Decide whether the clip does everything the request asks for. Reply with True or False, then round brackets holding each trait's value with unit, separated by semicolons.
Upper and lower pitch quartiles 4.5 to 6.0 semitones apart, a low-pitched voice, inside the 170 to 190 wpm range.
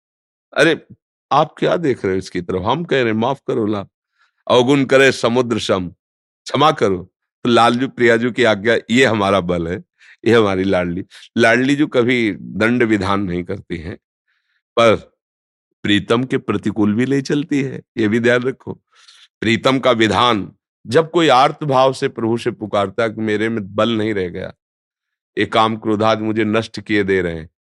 False (3.9 semitones; 110 Hz; 175 wpm)